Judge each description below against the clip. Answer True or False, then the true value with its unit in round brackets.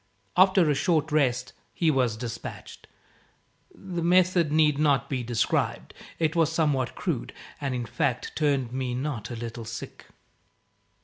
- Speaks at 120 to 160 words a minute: True (140 wpm)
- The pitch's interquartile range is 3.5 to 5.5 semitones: True (4.5 semitones)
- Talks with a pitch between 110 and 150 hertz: True (140 Hz)